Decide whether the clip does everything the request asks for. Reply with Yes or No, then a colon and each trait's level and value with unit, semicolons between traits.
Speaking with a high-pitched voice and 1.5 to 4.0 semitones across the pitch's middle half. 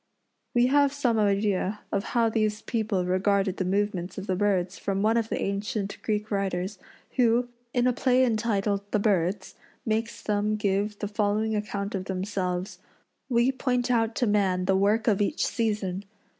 Yes: high, 210 Hz; narrow, 2.5 semitones